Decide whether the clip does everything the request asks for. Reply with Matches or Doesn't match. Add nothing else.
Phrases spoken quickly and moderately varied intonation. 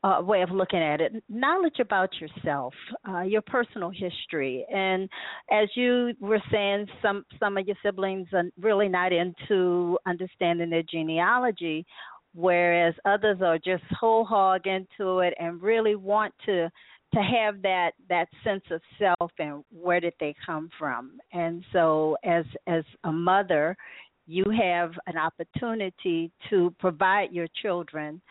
Doesn't match